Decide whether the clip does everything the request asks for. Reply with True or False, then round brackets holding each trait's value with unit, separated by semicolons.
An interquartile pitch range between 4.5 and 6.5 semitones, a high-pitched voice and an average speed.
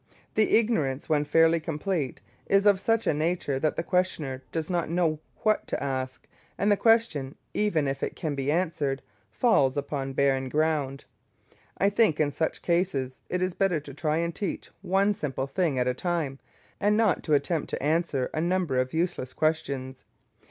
False (4.9 semitones; 155 Hz; 180 wpm)